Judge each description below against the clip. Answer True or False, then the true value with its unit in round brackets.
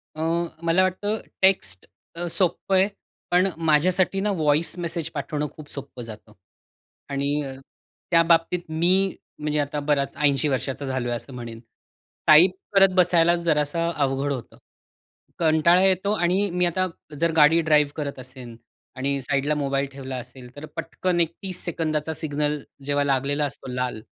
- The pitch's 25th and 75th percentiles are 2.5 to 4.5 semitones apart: True (3.6 semitones)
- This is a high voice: False (150 Hz)